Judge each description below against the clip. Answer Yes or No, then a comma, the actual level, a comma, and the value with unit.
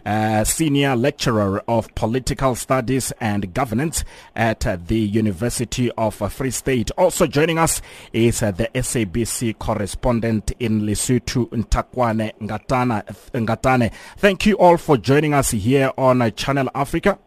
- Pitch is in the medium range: No, low, 120 Hz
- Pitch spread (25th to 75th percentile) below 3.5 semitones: No, average, 3.9 semitones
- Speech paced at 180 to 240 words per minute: No, slow, 135 wpm